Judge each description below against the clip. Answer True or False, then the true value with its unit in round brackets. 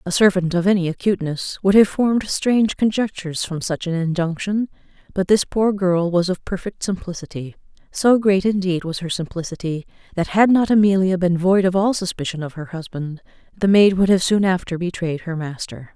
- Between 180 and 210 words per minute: True (185 wpm)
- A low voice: False (185 Hz)